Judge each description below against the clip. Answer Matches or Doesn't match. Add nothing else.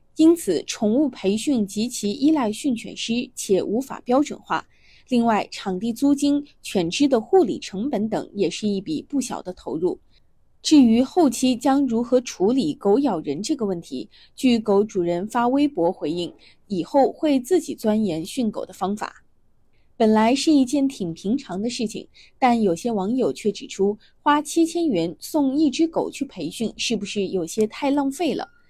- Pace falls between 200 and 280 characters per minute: Matches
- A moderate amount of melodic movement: Doesn't match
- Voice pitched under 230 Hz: Doesn't match